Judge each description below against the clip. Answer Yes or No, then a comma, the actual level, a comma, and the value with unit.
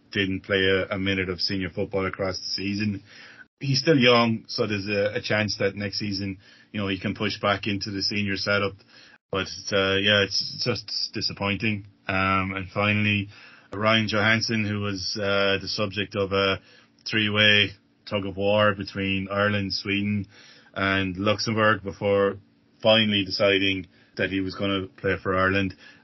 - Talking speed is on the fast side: No, average, 150 wpm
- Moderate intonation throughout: No, narrow, 1.4 semitones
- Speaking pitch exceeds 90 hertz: Yes, low, 100 Hz